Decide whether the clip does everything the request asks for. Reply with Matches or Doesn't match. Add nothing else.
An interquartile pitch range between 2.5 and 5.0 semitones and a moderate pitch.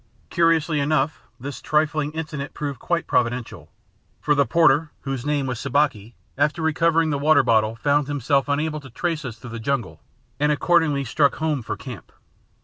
Matches